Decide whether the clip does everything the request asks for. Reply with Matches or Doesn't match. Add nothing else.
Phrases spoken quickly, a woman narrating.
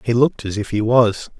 Doesn't match